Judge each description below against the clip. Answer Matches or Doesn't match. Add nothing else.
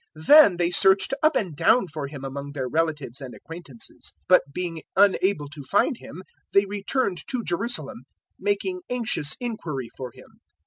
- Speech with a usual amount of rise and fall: Doesn't match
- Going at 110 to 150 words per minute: Doesn't match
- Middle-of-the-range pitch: Matches